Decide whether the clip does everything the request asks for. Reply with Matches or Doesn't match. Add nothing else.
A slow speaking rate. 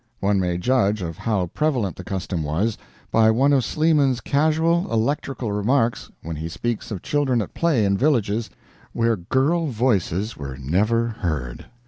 Doesn't match